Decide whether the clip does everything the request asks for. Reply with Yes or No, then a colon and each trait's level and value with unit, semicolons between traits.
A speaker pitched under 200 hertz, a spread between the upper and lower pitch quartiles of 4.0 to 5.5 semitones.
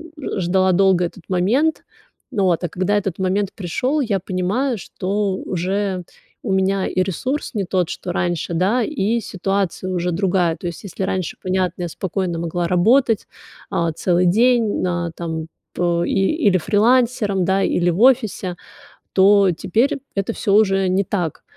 No: high, 190 Hz; average, 2.7 semitones